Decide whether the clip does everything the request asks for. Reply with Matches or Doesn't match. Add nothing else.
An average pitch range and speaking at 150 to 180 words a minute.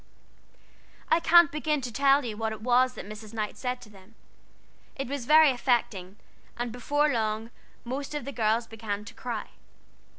Matches